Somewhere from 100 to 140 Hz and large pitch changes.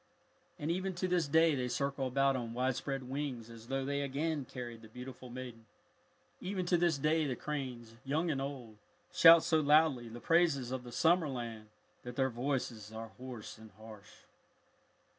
No: low, 135 Hz; average, 4.2 semitones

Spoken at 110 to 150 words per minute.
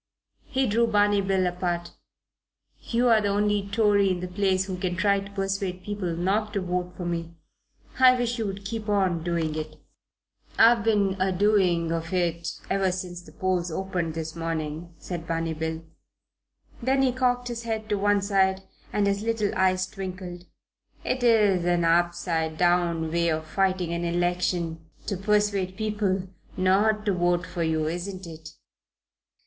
No: average, 160 wpm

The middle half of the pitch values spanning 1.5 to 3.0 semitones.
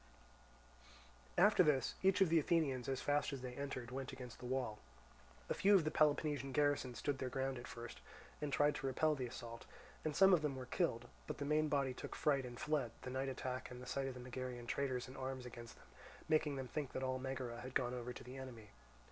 Yes: average, 2.7 semitones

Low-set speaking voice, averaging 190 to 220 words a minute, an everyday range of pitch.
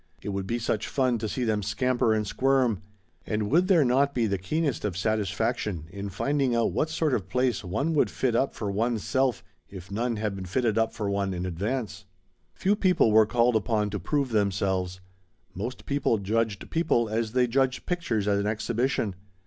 Yes: low, 115 Hz; average, 195 wpm; average, 4.1 semitones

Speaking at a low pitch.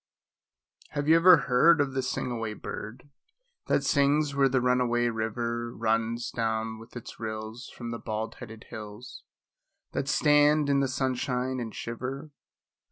Yes: low, 125 Hz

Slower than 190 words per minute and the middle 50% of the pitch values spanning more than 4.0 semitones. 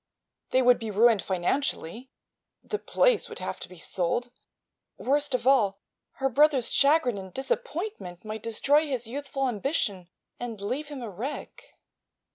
Yes: average, 145 wpm; average, 5.0 semitones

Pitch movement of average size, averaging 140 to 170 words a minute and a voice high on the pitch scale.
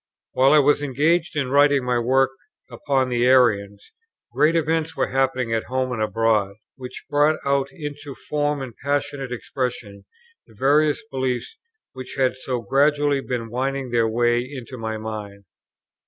No: average, 3.1 semitones; average, 155 wpm; low, 130 Hz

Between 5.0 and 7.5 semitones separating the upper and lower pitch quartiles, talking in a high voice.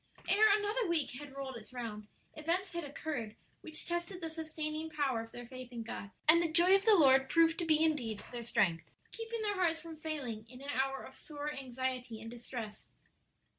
Yes: average, 5.3 semitones; very high, 295 Hz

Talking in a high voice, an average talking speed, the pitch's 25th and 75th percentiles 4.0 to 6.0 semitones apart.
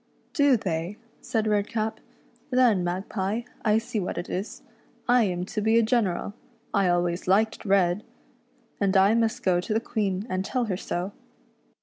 No: high, 210 Hz; average, 195 wpm; average, 3.5 semitones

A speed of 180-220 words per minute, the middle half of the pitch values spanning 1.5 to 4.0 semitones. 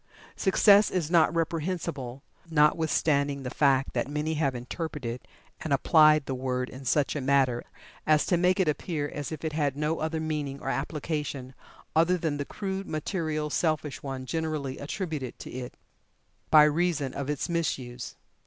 No: average, 160 wpm; average, 2.9 semitones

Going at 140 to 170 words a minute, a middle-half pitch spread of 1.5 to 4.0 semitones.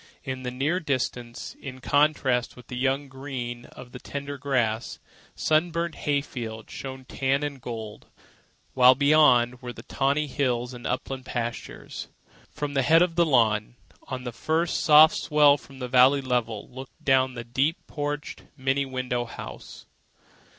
Yes: average, 155 wpm; average, 2.7 semitones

